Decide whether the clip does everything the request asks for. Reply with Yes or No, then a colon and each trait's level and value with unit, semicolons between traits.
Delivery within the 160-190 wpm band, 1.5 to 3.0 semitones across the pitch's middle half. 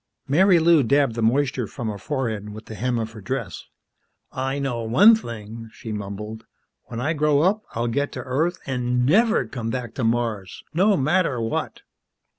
No: average, 175 wpm; average, 4.5 semitones